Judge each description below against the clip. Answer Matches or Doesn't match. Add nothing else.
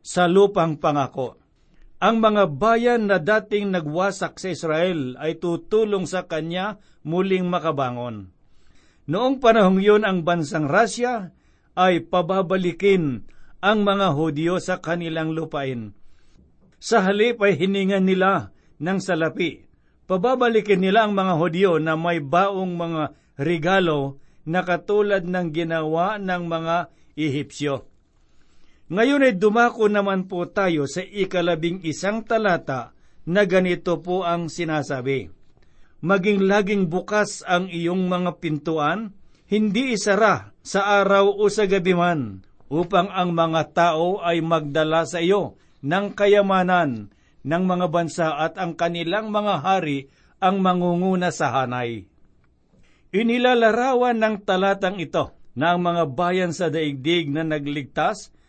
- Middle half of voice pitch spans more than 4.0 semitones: Doesn't match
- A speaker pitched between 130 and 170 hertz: Doesn't match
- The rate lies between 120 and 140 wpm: Matches